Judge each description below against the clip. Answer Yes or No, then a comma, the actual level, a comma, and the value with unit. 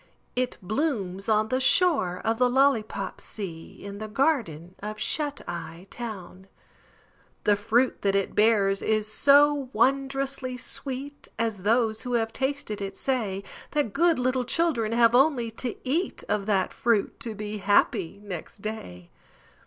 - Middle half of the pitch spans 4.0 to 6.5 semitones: Yes, average, 4.7 semitones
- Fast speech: No, average, 145 wpm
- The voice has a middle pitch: No, high, 225 Hz